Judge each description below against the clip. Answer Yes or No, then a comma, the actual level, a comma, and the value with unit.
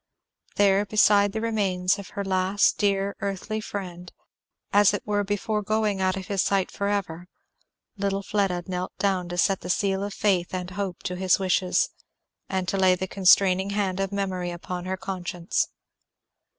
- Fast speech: No, average, 165 wpm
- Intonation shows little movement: Yes, narrow, 1.7 semitones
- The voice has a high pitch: Yes, high, 195 Hz